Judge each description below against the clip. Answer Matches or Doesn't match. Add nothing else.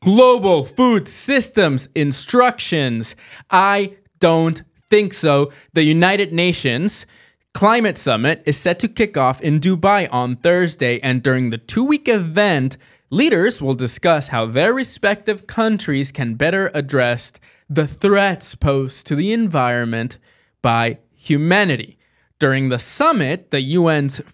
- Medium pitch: Matches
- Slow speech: Matches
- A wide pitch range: Matches